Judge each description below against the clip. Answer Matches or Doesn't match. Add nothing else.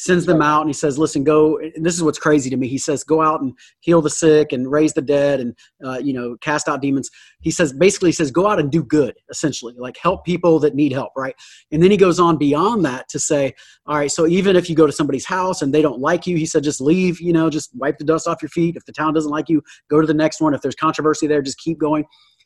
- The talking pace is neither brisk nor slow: Doesn't match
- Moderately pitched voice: Matches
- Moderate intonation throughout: Doesn't match